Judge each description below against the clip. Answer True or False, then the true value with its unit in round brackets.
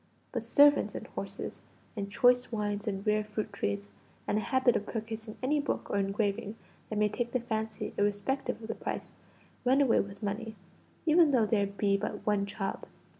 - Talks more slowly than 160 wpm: False (180 wpm)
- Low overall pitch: False (215 Hz)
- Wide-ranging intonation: False (3.0 semitones)